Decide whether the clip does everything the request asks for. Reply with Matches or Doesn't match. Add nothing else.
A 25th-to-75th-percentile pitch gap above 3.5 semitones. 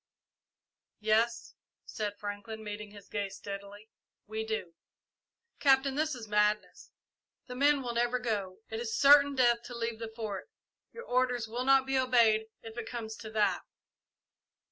Doesn't match